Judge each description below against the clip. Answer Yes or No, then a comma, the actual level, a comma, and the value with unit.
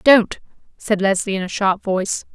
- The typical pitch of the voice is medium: No, high, 200 Hz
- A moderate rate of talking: Yes, average, 180 wpm